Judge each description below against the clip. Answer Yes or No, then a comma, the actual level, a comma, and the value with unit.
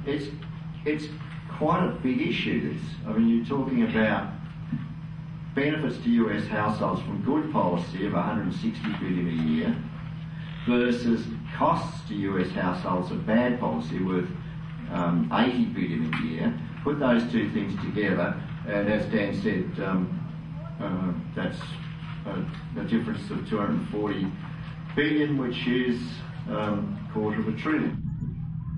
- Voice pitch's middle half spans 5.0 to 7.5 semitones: Yes, wide, 5.4 semitones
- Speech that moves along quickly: No, slow, 135 wpm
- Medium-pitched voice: Yes, medium, 150 Hz